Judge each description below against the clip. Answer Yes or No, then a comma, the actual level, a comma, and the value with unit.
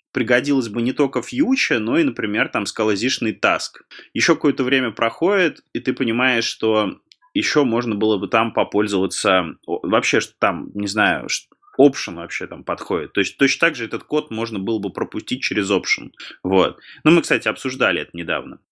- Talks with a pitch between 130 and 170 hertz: No, low, 120 Hz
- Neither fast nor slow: No, fast, 175 wpm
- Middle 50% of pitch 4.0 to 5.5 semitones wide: Yes, average, 4.7 semitones